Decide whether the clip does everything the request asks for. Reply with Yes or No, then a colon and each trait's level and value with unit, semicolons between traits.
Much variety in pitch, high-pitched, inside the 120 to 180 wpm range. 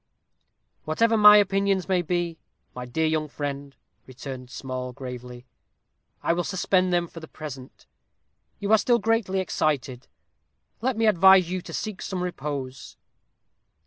No: wide, 6.2 semitones; medium, 170 Hz; average, 140 wpm